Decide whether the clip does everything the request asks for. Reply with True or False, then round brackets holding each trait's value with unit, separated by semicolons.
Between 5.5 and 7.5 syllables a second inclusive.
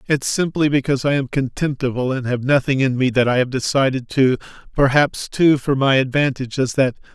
True (5.6 syllables/s)